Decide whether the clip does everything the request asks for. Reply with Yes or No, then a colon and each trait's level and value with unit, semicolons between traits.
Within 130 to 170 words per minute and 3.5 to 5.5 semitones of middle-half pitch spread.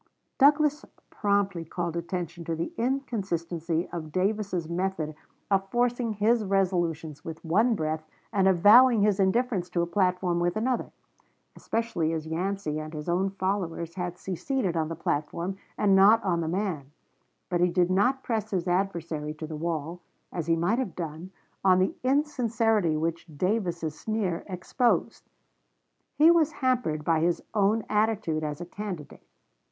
Yes: average, 150 wpm; average, 4.4 semitones